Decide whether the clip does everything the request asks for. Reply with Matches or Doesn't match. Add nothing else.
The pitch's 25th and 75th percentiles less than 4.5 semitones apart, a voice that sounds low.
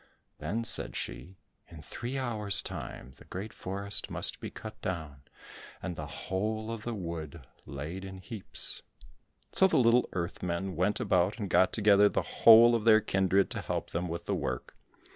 Matches